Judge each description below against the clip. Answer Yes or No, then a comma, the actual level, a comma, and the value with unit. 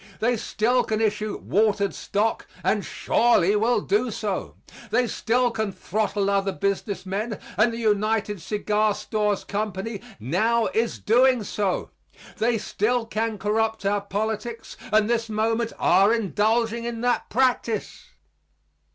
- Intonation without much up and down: Yes, narrow, 1.9 semitones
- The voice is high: Yes, high, 215 Hz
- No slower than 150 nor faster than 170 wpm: No, slow, 135 wpm